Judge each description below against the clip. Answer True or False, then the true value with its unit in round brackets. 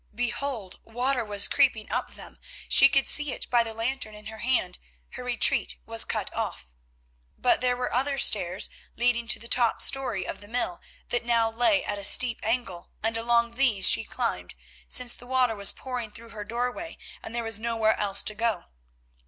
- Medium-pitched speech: False (235 Hz)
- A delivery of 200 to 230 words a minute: False (185 wpm)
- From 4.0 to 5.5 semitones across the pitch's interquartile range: False (2.6 semitones)